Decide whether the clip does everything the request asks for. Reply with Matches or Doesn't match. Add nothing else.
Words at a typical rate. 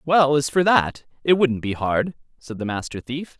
Doesn't match